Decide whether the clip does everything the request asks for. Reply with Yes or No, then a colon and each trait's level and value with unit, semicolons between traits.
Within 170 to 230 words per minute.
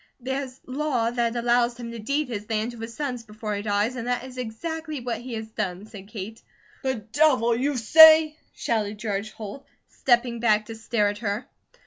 Yes: average, 190 wpm